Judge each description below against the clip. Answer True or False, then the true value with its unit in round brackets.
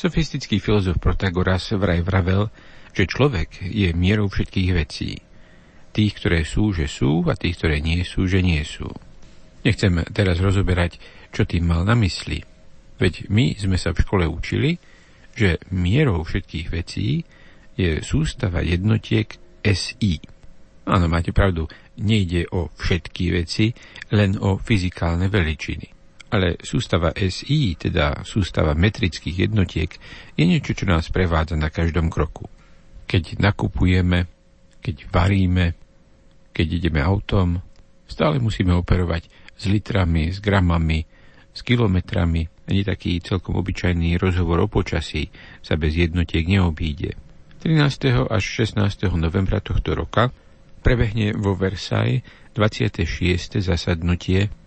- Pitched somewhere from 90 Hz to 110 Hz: True (95 Hz)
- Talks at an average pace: True (120 wpm)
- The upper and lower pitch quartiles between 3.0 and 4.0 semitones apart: True (3.5 semitones)